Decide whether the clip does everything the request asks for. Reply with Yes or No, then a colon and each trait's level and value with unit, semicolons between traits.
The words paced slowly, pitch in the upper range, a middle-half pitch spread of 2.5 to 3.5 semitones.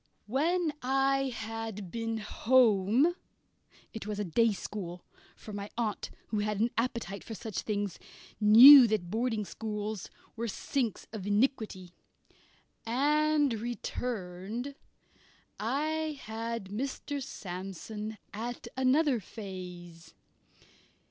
No: slow, 105 wpm; high, 225 Hz; average, 3.9 semitones